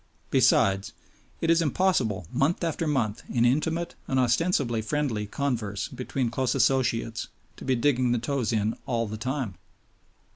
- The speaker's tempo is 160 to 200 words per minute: No, average, 145 wpm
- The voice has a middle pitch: No, low, 125 Hz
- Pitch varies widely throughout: No, average, 4.2 semitones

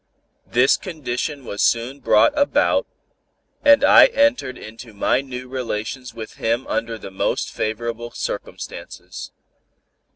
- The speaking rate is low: Yes, slow, 120 wpm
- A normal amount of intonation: Yes, average, 3.3 semitones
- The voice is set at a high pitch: No, low, 125 Hz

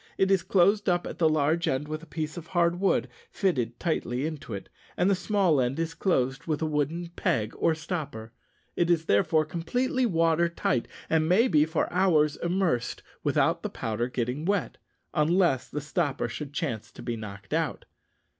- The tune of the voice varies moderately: Yes, average, 4.4 semitones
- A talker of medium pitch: Yes, medium, 160 Hz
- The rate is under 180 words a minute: No, average, 185 wpm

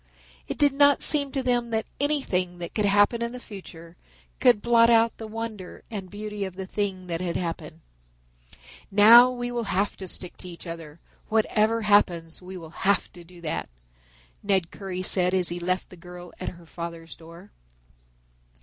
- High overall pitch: Yes, high, 195 Hz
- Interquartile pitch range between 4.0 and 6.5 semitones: Yes, average, 4.4 semitones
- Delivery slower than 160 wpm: No, average, 180 wpm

